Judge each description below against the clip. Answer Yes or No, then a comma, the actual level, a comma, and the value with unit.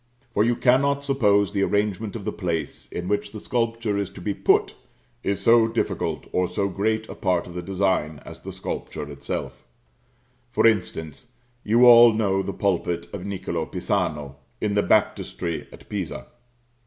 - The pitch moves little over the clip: No, average, 3.8 semitones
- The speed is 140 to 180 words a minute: Yes, average, 165 wpm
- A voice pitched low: Yes, low, 100 Hz